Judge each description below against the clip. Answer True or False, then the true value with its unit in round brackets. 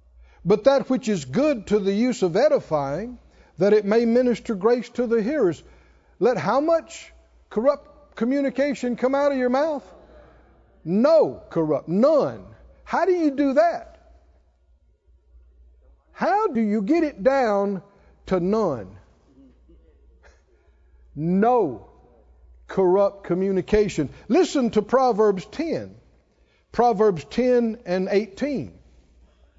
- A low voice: False (210 Hz)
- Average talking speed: False (110 wpm)